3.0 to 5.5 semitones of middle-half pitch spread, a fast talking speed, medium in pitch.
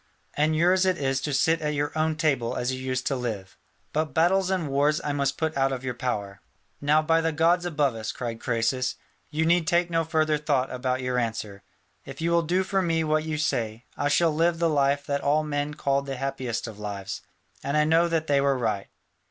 Yes: average, 3.9 semitones; fast, 225 wpm; medium, 145 Hz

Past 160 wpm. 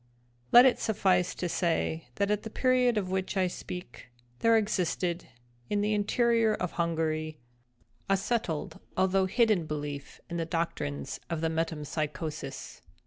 No: average, 140 wpm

